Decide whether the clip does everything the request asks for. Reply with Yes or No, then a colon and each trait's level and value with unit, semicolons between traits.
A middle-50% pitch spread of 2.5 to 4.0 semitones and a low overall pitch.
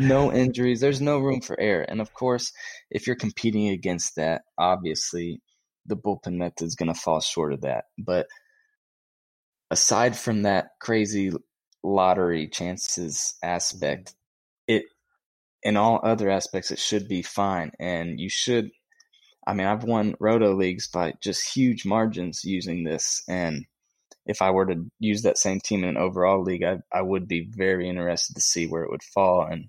No: average, 4.4 semitones; very low, 95 Hz